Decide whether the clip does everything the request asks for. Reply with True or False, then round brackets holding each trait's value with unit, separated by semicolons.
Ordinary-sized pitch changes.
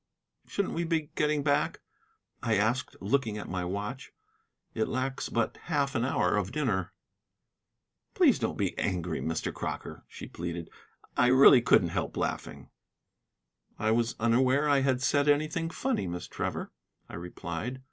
False (5.9 semitones)